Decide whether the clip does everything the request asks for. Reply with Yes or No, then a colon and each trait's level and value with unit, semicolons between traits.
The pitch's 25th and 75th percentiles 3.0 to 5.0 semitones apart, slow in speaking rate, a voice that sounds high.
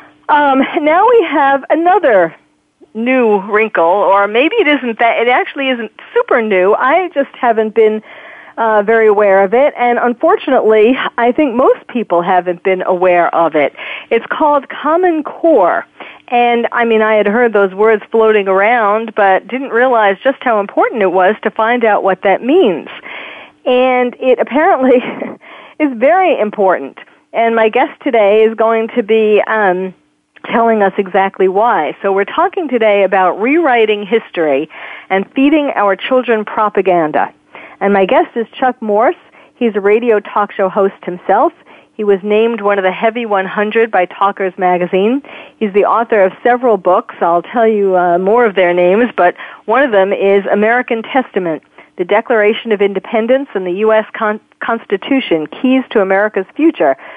No: average, 4.5 semitones; average, 160 wpm; high, 220 Hz